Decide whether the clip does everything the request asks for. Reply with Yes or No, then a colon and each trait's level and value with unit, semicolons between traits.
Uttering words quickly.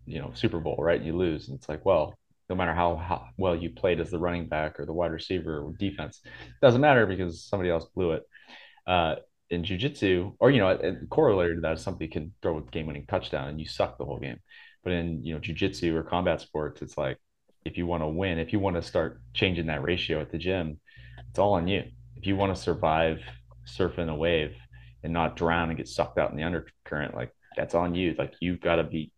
Yes: fast, 245 wpm